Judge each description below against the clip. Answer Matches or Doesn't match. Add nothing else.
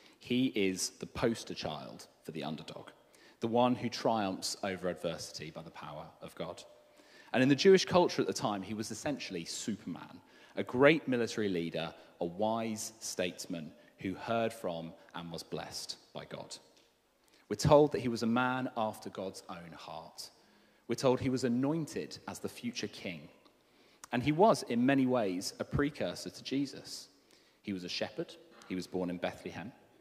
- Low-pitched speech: Matches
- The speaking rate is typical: Matches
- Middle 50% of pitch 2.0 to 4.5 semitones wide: Doesn't match